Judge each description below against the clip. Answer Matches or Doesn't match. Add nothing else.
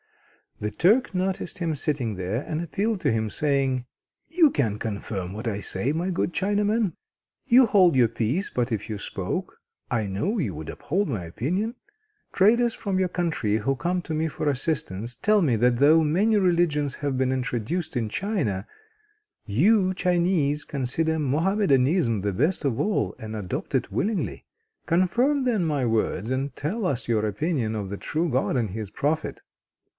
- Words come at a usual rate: Matches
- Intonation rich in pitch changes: Matches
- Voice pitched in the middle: Matches